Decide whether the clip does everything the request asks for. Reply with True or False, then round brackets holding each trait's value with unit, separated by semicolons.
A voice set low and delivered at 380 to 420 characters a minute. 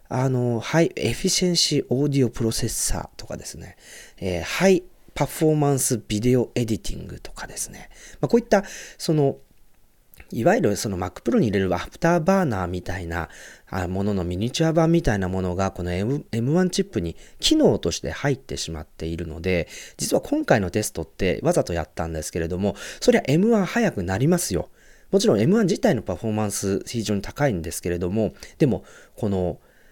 True (115 Hz; 395 characters per minute)